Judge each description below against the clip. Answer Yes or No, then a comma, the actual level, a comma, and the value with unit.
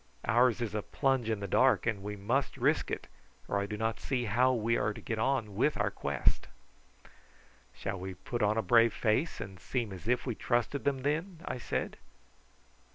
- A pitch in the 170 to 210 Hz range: No, low, 115 Hz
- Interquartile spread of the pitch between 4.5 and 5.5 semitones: No, average, 3.6 semitones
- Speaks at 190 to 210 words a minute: Yes, average, 200 wpm